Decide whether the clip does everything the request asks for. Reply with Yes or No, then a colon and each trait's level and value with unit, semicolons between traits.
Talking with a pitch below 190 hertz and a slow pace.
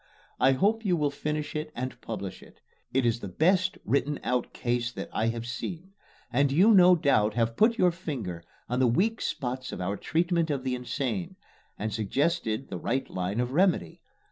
No: low, 135 Hz; average, 190 wpm